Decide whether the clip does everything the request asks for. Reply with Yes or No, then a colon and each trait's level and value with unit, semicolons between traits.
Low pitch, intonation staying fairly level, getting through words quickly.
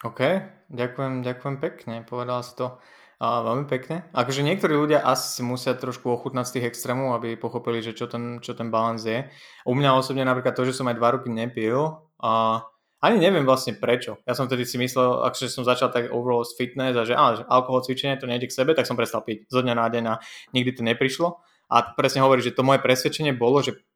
Yes: low, 125 Hz; narrow, 1.8 semitones; fast, 225 wpm